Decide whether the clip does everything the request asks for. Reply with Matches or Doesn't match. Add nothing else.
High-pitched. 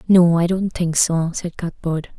Doesn't match